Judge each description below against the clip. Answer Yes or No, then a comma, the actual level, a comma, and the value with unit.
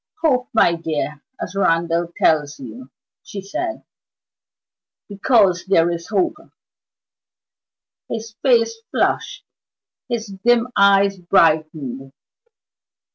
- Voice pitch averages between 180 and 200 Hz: Yes, high, 190 Hz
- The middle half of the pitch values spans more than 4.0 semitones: Yes, wide, 5.5 semitones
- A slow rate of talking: Yes, slow, 90 wpm